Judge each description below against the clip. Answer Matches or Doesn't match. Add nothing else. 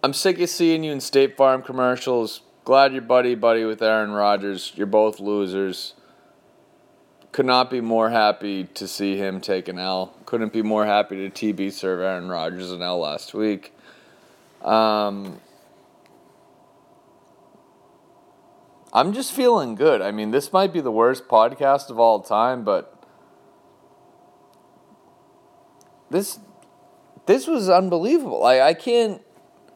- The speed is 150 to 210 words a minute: Doesn't match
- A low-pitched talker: Matches